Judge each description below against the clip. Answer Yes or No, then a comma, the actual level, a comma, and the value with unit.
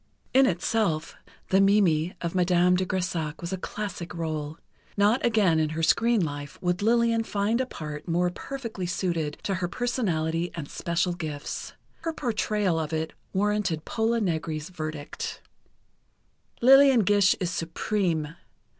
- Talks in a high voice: No, medium, 180 Hz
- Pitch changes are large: No, average, 4.7 semitones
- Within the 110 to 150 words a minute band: Yes, average, 140 wpm